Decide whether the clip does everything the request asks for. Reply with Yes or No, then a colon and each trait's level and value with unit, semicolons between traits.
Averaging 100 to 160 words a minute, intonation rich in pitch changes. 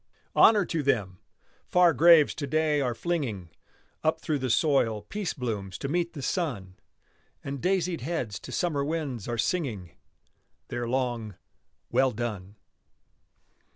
Yes: slow, 135 wpm; wide, 6.4 semitones